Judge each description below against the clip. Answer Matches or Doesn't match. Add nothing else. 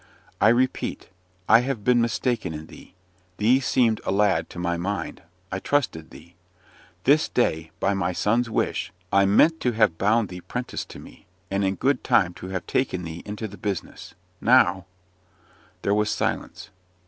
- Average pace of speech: Matches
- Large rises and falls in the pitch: Doesn't match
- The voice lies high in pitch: Doesn't match